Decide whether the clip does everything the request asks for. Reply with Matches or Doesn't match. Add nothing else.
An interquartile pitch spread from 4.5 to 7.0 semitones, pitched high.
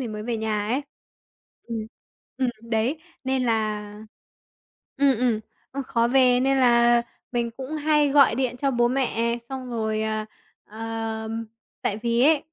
Doesn't match